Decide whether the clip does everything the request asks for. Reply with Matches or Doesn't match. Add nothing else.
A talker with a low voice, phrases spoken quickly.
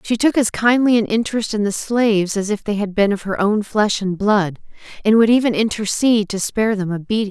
Doesn't match